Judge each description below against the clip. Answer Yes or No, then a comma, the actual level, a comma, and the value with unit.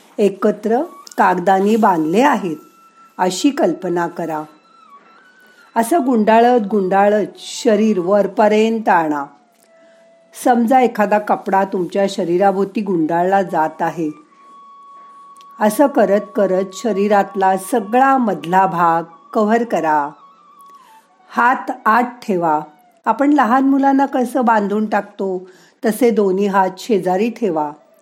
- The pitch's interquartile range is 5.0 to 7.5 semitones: Yes, wide, 5.6 semitones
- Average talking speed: Yes, average, 95 wpm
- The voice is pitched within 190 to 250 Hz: Yes, high, 215 Hz